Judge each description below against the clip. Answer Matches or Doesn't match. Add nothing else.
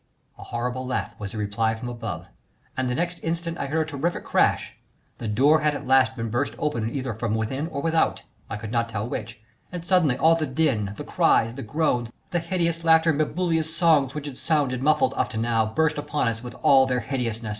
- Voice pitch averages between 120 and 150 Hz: Matches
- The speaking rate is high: Matches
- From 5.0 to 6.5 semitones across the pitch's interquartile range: Matches